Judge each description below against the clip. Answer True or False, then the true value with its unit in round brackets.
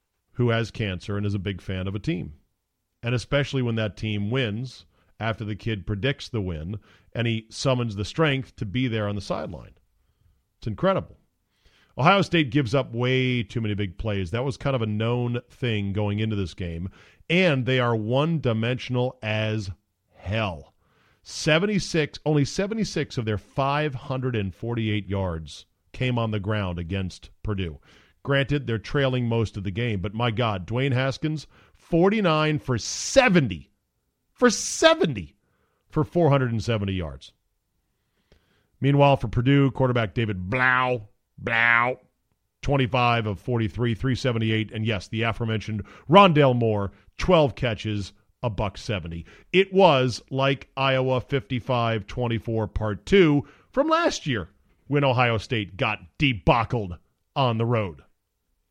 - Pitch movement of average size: True (4.6 semitones)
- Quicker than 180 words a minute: False (145 wpm)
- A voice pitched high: False (115 Hz)